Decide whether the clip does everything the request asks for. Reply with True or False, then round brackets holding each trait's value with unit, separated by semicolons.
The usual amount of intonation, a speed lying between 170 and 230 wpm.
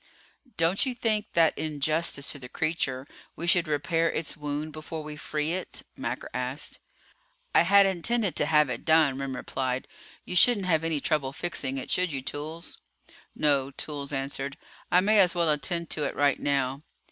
True (3.4 semitones; 180 wpm)